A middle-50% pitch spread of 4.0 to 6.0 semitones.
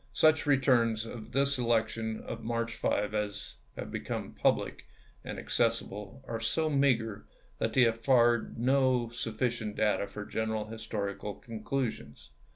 No: narrow, 2.6 semitones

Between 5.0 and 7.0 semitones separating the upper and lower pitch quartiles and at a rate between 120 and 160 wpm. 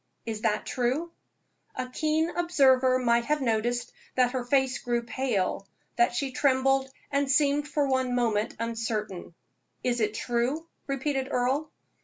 No: average, 2.8 semitones; average, 140 wpm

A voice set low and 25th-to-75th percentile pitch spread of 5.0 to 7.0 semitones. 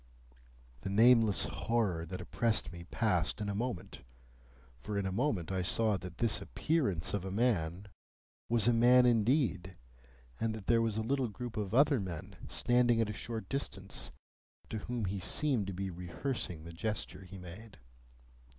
No: low, 105 Hz; average, 4.2 semitones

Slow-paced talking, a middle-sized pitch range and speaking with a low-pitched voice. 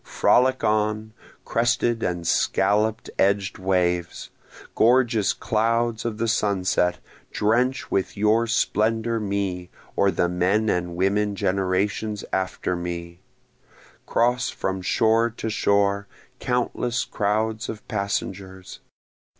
Yes: slow, 105 wpm; average, 3.1 semitones; low, 105 Hz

